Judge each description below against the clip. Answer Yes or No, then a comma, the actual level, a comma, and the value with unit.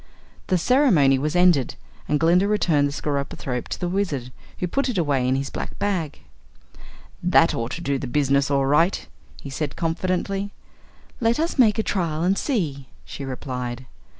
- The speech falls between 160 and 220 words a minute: Yes, average, 170 wpm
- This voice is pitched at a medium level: Yes, medium, 155 Hz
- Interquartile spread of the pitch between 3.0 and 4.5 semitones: No, average, 5.2 semitones